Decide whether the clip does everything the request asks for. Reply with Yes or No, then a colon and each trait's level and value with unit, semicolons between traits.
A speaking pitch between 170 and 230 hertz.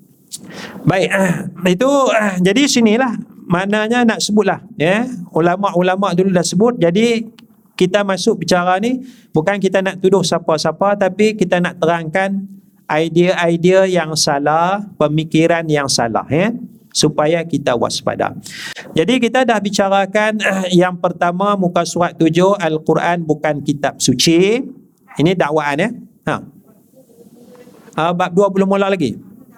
Yes: high, 190 Hz